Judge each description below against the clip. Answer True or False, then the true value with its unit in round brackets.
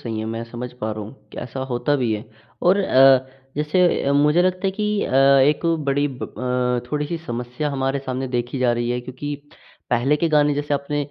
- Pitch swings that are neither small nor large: True (3.2 semitones)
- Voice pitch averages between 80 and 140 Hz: True (135 Hz)